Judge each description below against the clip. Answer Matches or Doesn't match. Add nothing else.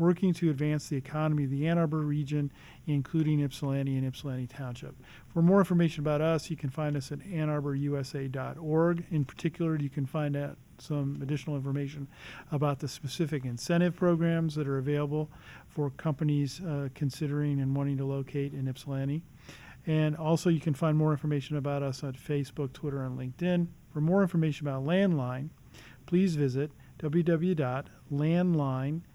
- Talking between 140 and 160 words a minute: Matches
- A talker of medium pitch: Matches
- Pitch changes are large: Doesn't match